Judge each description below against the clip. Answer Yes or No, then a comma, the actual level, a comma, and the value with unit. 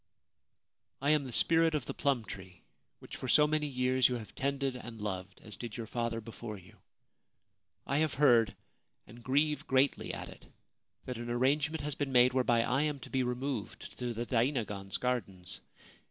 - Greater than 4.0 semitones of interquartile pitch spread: No, average, 3.5 semitones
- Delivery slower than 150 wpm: No, average, 190 wpm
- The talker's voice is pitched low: Yes, low, 125 Hz